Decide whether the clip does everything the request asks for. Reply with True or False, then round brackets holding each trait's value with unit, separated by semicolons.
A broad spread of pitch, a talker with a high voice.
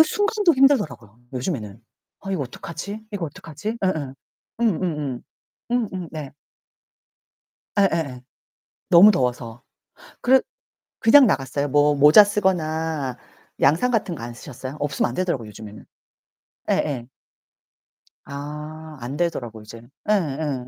False (6.8 semitones; 150 Hz)